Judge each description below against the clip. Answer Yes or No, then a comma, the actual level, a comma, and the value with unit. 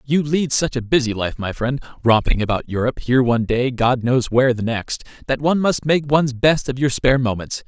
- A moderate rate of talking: No, fast, 225 wpm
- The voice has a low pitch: Yes, low, 125 Hz